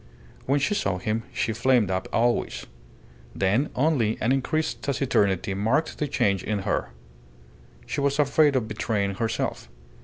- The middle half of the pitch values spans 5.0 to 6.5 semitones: Yes, wide, 5.6 semitones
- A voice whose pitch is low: Yes, low, 115 Hz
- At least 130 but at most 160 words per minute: Yes, average, 145 wpm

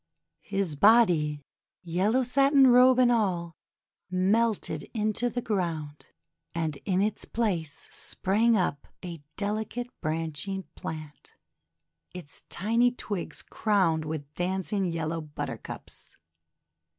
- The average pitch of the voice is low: No, high, 190 Hz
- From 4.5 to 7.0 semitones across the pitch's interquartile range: Yes, wide, 5.6 semitones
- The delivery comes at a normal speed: No, slow, 100 wpm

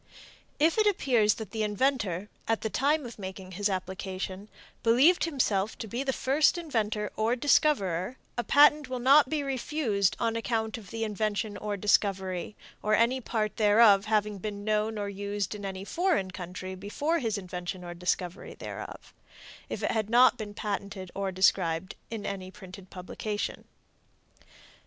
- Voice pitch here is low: No, high, 210 Hz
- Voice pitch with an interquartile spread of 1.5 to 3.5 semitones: No, average, 3.9 semitones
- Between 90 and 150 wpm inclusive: No, average, 160 wpm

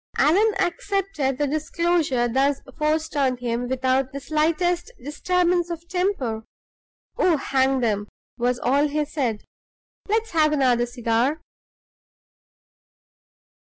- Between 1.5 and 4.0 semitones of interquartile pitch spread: No, average, 5.1 semitones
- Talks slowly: Yes, slow, 110 wpm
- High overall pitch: Yes, very high, 290 Hz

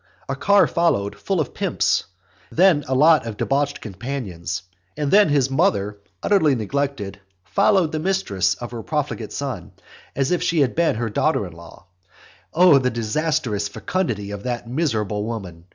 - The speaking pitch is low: Yes, low, 130 Hz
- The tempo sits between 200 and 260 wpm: No, average, 160 wpm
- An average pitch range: No, wide, 7.4 semitones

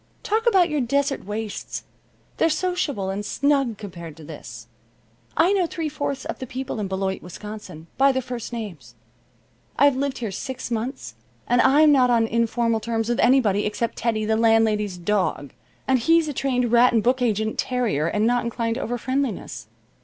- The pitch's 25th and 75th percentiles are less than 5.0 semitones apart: Yes, average, 4.2 semitones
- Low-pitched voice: No, high, 235 Hz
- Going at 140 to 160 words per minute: No, average, 175 wpm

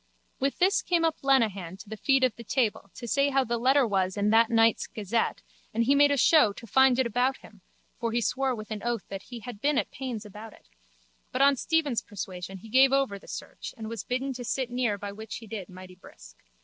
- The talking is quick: Yes, fast, 240 wpm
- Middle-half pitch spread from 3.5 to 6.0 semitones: Yes, average, 4.3 semitones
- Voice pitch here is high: Yes, high, 235 Hz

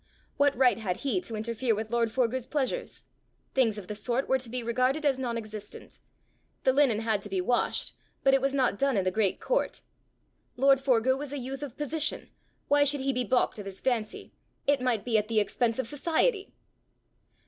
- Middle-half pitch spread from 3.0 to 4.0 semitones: Yes, average, 3.6 semitones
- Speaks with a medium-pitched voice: No, very high, 250 Hz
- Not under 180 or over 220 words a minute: Yes, fast, 205 wpm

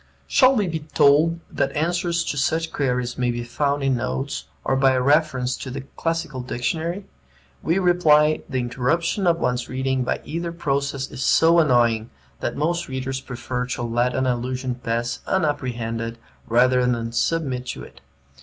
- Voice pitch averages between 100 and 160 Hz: Yes, low, 135 Hz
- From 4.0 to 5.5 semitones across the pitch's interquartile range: Yes, average, 4.6 semitones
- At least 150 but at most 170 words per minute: Yes, average, 165 wpm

